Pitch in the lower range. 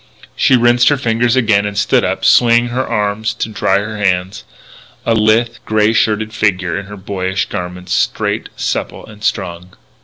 Yes: low, 105 Hz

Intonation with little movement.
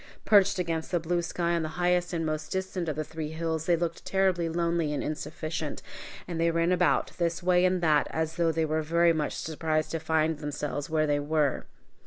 Yes: narrow, 1.8 semitones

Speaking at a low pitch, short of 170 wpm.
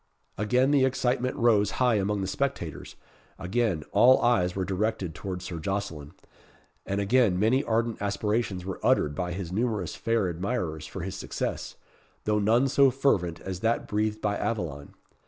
Yes: low, 100 Hz; average, 155 wpm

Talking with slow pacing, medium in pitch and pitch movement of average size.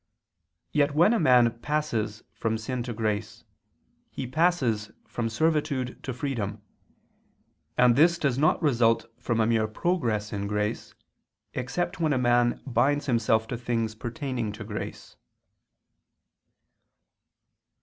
No: slow, 125 wpm; low, 120 Hz; average, 4.4 semitones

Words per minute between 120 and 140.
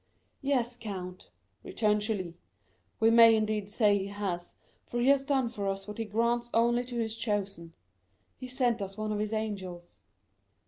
No: average, 170 wpm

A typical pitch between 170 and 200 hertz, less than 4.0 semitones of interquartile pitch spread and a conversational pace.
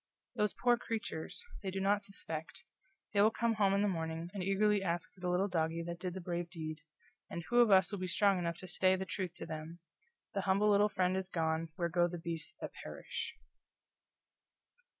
No: medium, 185 Hz; average, 3.0 semitones; fast, 210 wpm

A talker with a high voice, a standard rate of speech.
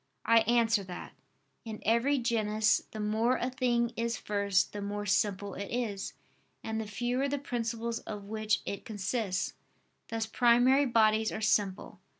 Yes: high, 220 Hz; average, 155 wpm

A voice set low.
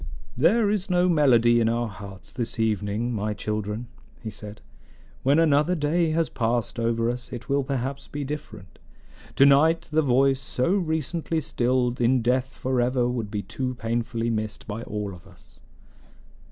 Yes: low, 125 Hz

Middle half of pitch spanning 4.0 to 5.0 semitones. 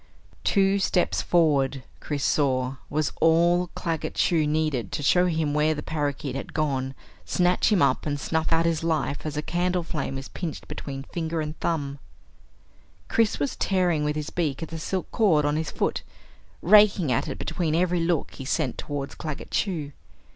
No: average, 3.1 semitones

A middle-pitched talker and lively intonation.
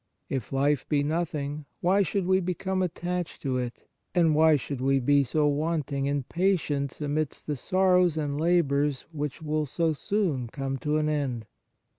No: medium, 150 Hz; average, 3.4 semitones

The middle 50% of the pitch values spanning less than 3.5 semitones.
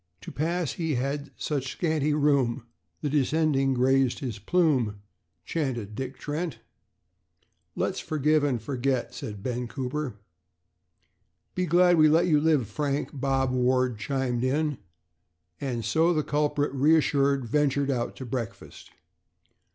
Yes: average, 3.1 semitones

